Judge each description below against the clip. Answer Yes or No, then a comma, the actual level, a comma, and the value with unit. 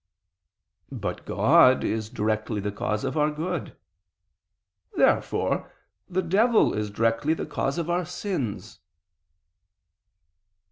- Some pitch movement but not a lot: No, wide, 8.3 semitones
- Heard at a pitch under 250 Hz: Yes, low, 135 Hz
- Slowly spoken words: Yes, slow, 105 wpm